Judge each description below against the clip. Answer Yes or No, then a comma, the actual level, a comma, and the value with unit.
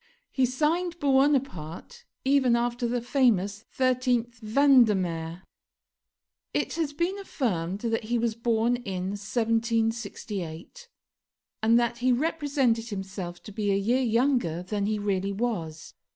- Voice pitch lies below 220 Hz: No, high, 230 Hz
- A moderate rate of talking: No, slow, 125 wpm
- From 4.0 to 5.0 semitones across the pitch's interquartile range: Yes, average, 4.4 semitones